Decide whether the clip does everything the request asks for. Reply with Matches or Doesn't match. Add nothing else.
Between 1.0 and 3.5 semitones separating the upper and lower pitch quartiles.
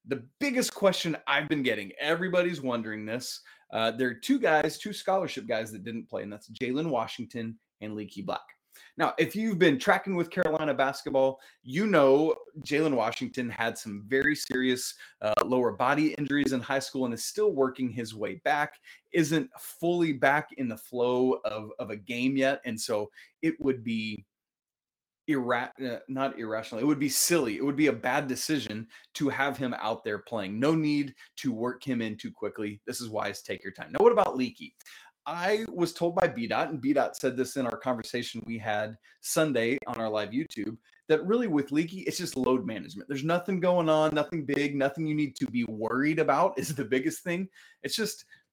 Doesn't match